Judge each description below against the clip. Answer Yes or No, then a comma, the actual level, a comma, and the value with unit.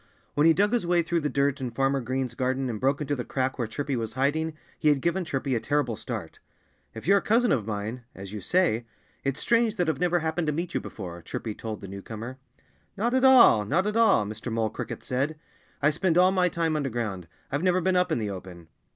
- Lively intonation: Yes, wide, 7.3 semitones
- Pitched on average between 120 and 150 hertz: Yes, medium, 140 Hz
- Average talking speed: No, fast, 235 wpm